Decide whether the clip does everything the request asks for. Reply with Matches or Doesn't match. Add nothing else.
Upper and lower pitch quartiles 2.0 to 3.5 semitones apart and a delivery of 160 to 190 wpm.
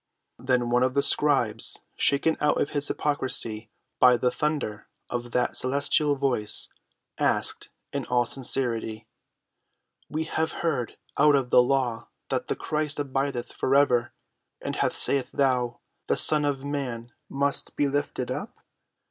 Doesn't match